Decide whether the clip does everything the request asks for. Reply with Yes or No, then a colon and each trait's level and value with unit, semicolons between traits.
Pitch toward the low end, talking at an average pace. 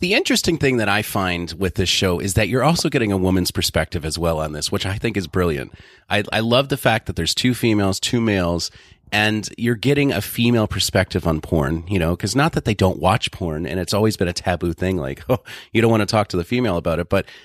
No: low, 100 Hz; fast, 255 wpm